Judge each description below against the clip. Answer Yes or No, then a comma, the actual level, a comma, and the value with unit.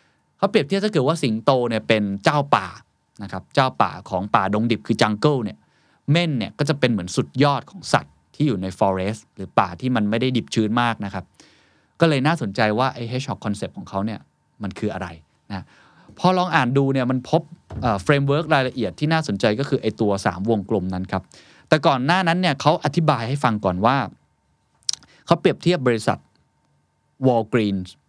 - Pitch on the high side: No, low, 125 Hz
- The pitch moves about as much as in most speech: No, wide, 6.3 semitones